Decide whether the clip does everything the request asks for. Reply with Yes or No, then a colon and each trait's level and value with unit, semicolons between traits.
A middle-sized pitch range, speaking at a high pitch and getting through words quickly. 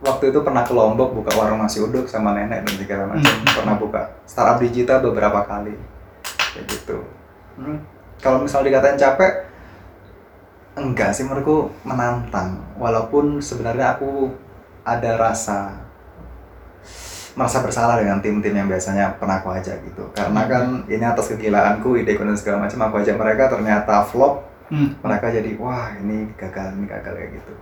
No: average, 4.1 semitones; low, 110 Hz; fast, 150 wpm